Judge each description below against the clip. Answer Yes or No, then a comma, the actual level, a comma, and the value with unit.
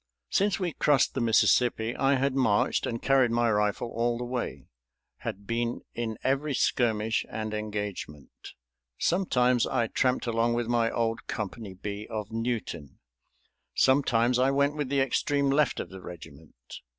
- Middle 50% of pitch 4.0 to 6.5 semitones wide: No, average, 3.5 semitones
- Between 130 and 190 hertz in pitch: No, low, 120 Hz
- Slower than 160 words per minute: Yes, average, 150 wpm